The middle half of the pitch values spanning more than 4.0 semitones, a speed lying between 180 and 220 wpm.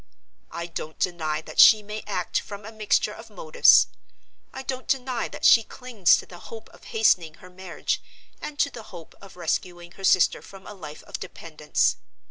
Yes: average, 4.7 semitones; average, 185 wpm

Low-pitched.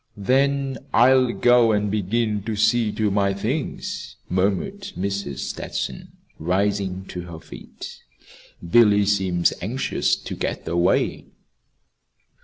Yes: low, 105 Hz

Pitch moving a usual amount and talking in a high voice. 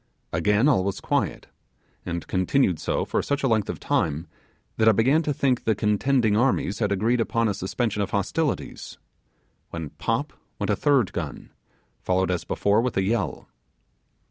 No: average, 4.8 semitones; low, 105 Hz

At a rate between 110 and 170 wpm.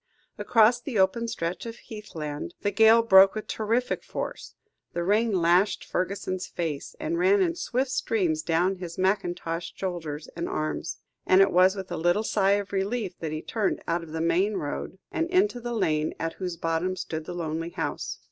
No: average, 185 wpm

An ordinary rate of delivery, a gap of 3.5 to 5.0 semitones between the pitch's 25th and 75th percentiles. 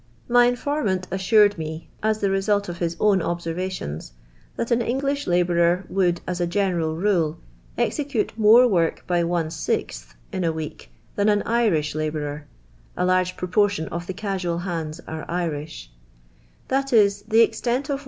Yes: average, 165 wpm; average, 4.3 semitones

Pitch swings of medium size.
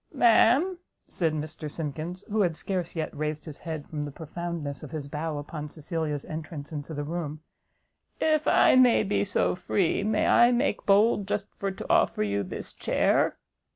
Yes: average, 5.0 semitones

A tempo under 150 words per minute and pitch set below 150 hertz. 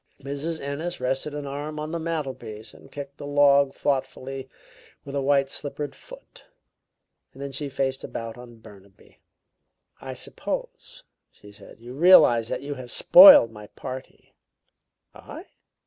Yes: average, 140 wpm; medium, 140 Hz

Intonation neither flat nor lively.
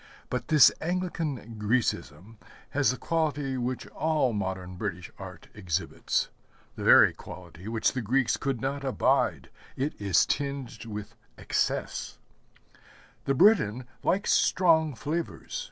No: wide, 5.9 semitones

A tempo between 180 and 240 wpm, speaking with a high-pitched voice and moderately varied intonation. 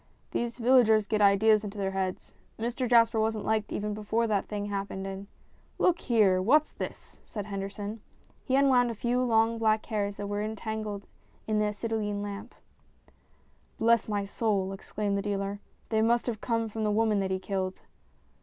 No: average, 185 wpm; high, 215 Hz; narrow, 2.1 semitones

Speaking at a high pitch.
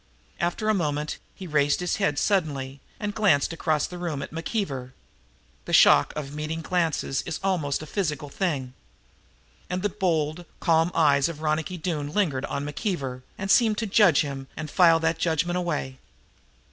No: medium, 160 Hz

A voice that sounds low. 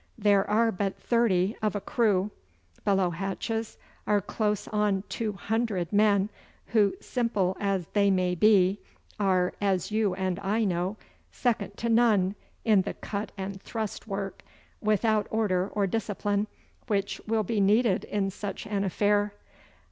No: high, 205 Hz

